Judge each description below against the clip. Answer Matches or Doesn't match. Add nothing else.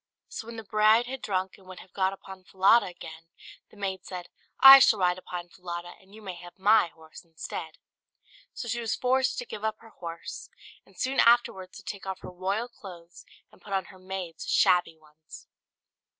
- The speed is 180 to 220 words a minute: Matches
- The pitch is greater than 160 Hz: Matches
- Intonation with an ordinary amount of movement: Matches